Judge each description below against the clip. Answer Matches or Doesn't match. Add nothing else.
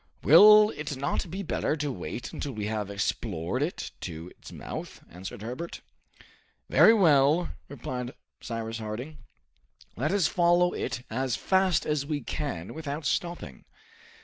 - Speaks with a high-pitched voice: Doesn't match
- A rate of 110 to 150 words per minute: Matches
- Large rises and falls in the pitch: Matches